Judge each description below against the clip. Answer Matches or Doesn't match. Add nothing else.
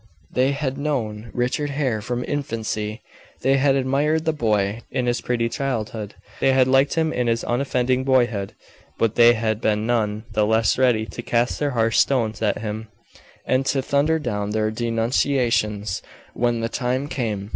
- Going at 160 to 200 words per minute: Matches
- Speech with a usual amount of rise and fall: Matches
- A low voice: Matches